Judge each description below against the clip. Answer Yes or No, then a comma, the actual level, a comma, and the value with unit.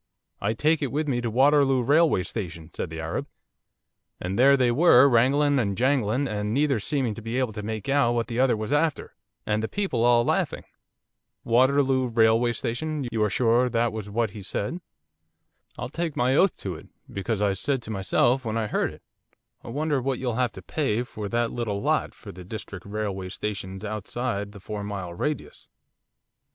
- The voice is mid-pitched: No, low, 120 Hz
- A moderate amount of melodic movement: Yes, average, 4.3 semitones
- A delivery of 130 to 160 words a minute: No, average, 190 wpm